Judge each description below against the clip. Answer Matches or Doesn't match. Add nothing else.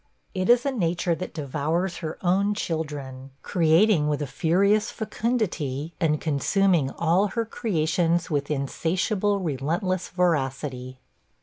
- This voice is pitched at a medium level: Matches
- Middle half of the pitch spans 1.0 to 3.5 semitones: Doesn't match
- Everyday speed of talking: Doesn't match